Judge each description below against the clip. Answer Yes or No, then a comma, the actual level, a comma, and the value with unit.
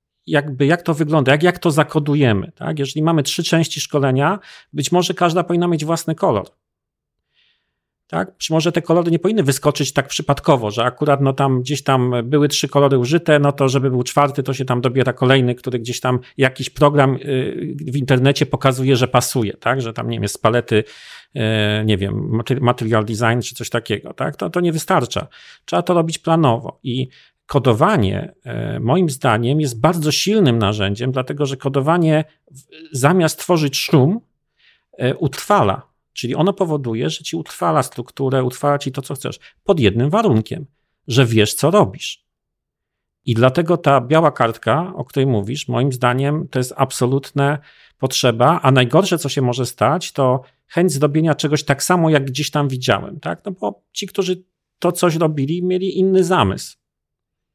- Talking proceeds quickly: Yes, fast, 165 wpm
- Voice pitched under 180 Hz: Yes, medium, 140 Hz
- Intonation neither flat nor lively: Yes, average, 4.1 semitones